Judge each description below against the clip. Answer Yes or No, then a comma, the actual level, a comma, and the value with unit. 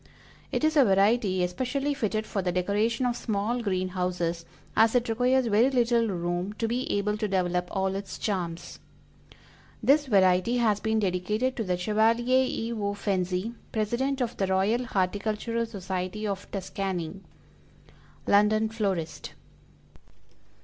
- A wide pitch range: No, average, 3.9 semitones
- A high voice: Yes, high, 210 Hz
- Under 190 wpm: Yes, average, 140 wpm